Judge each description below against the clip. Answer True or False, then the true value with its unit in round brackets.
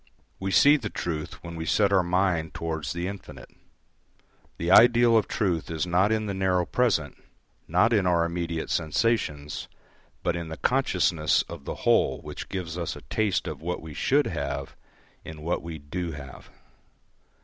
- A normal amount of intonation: True (3.6 semitones)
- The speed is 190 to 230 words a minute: False (170 wpm)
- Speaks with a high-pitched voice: False (85 Hz)